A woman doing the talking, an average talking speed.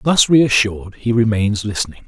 No: male; average, 145 wpm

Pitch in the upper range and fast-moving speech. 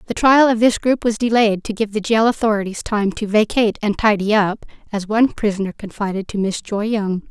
Yes: high, 210 Hz; fast, 215 wpm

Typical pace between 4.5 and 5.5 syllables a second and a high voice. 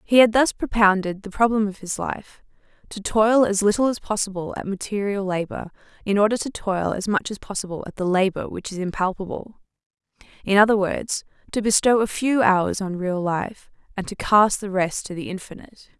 Yes: 5.3 syllables/s; high, 200 Hz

